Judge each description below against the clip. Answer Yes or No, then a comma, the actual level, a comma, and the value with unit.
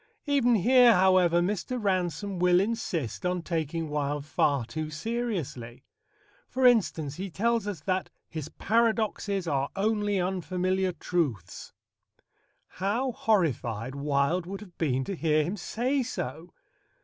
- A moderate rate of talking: No, slow, 125 wpm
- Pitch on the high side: No, medium, 180 Hz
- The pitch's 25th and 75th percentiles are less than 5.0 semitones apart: No, wide, 5.4 semitones